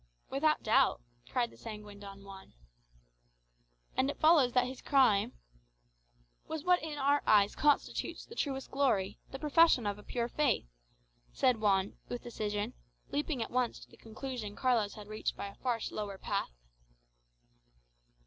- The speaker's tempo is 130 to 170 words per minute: Yes, average, 155 wpm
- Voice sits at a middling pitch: No, high, 240 Hz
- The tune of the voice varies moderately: Yes, average, 5.0 semitones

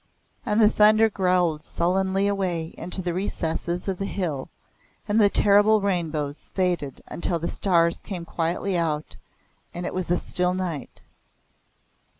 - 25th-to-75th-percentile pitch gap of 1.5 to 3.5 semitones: Yes, average, 2.8 semitones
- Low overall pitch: No, medium, 180 Hz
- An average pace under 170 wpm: Yes, average, 145 wpm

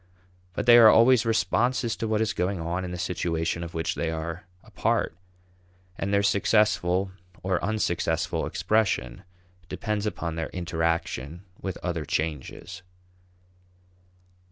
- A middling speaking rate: No, slow, 130 wpm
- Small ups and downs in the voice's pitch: No, average, 4.4 semitones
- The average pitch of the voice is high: No, very low, 90 Hz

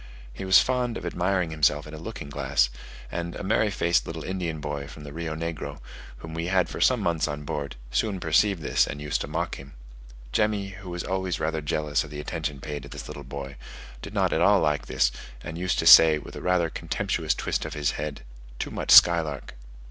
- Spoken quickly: Yes, fast, 215 wpm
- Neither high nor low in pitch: No, very low, 80 Hz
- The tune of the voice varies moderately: Yes, average, 3.7 semitones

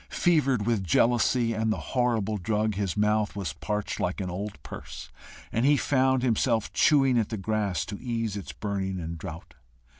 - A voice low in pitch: Yes, low, 110 Hz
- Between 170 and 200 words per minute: Yes, average, 175 wpm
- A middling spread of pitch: Yes, average, 3.4 semitones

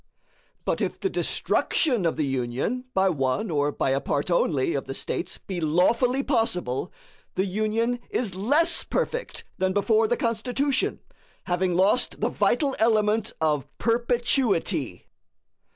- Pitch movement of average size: No, wide, 7.0 semitones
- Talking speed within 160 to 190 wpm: No, slow, 135 wpm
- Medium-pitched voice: No, high, 200 Hz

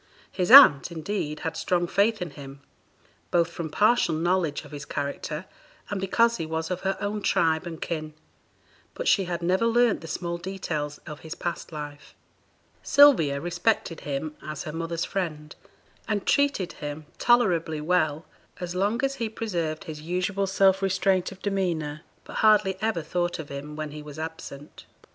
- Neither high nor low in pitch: Yes, medium, 170 Hz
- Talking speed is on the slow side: No, average, 165 wpm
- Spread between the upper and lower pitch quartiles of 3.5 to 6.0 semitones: Yes, average, 4.0 semitones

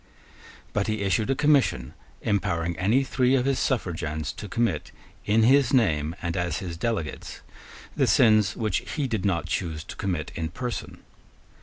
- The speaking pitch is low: Yes, low, 100 Hz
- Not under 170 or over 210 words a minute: No, average, 160 wpm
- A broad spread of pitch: Yes, wide, 6.2 semitones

